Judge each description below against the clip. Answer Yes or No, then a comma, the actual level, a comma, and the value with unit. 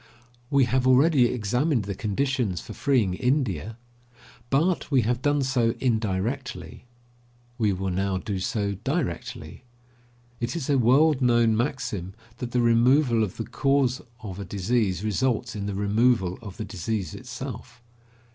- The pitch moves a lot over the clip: No, average, 4.4 semitones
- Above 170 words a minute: No, average, 145 wpm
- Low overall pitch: Yes, low, 120 Hz